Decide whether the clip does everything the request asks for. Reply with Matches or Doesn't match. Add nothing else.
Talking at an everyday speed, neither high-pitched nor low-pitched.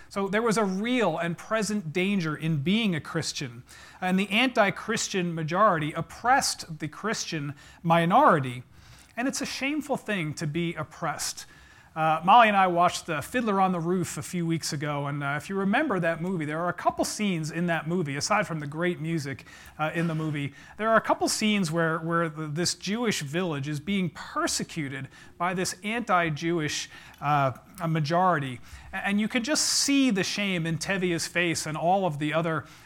Matches